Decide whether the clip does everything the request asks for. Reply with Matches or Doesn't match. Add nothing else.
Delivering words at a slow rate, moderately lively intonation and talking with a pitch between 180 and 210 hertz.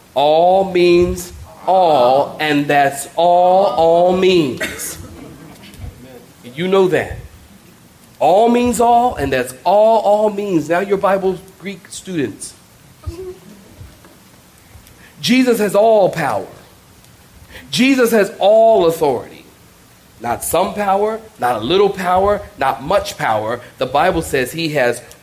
Matches